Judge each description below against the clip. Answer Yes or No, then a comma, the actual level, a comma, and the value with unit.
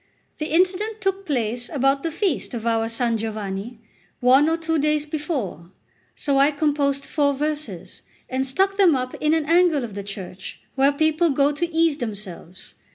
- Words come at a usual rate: Yes, average, 170 wpm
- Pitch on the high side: Yes, very high, 285 Hz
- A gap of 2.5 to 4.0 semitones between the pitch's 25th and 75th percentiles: No, average, 5.2 semitones